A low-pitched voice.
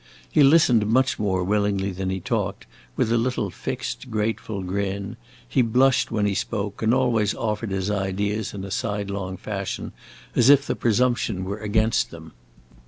Yes: low, 105 Hz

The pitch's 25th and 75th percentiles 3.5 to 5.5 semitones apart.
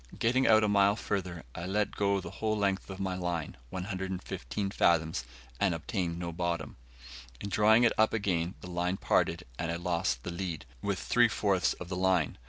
No: average, 2.8 semitones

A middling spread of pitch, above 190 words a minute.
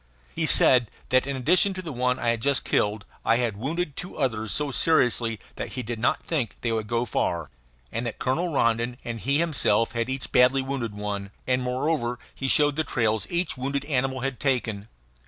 Yes: average, 3.3 semitones; average, 200 wpm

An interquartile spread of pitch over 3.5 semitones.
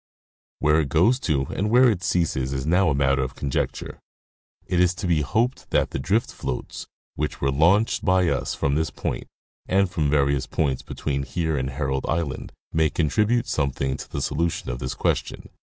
Yes: average, 4.8 semitones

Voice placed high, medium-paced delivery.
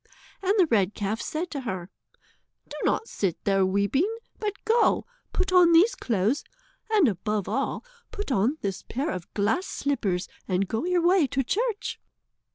Yes: very high, 270 Hz; average, 165 wpm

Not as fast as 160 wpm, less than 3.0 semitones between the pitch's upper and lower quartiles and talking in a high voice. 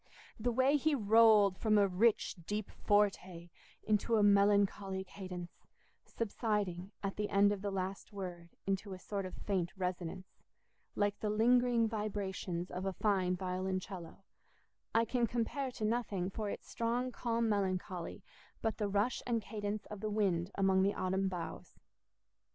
Yes: average, 150 wpm; narrow, 2.6 semitones; high, 200 Hz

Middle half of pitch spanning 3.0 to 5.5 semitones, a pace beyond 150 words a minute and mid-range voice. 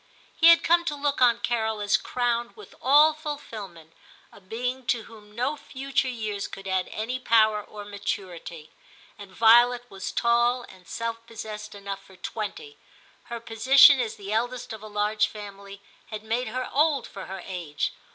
No: average, 3.6 semitones; average, 170 wpm; high, 225 Hz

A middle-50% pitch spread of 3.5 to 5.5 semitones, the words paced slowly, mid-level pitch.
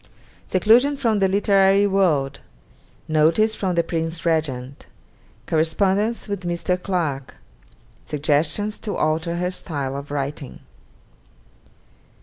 Yes: average, 4.7 semitones; slow, 105 wpm; medium, 170 Hz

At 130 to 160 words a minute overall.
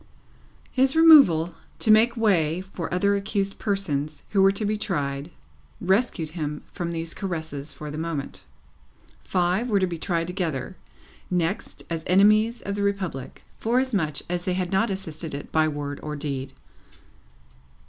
Yes: average, 150 wpm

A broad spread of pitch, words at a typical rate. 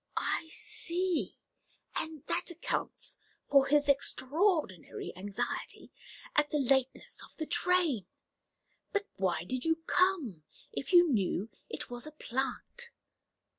No: wide, 6.1 semitones; slow, 120 wpm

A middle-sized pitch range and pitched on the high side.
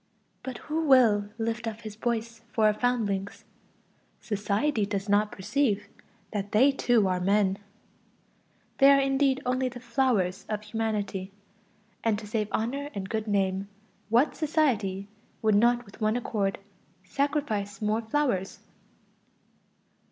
Yes: average, 3.7 semitones; high, 220 Hz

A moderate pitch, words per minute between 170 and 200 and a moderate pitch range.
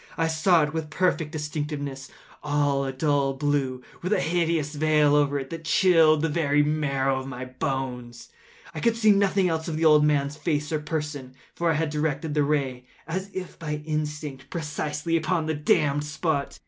No: medium, 150 Hz; average, 185 wpm; narrow, 2.3 semitones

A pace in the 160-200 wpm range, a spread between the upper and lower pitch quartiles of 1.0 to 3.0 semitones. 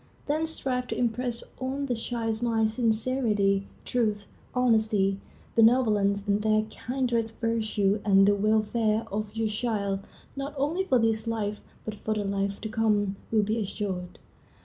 No: average, 150 wpm; average, 2.7 semitones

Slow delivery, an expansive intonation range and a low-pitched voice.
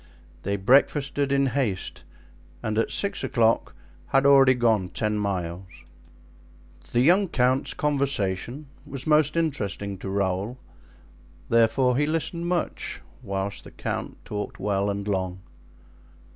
Yes: slow, 120 wpm; wide, 5.9 semitones; low, 120 Hz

